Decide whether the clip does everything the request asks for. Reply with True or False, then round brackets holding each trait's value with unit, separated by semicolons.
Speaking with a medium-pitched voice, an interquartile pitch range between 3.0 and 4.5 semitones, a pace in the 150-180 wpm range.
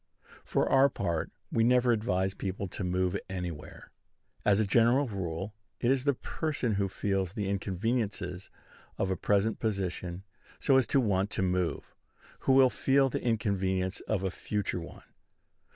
False (100 Hz; 4.1 semitones; 155 wpm)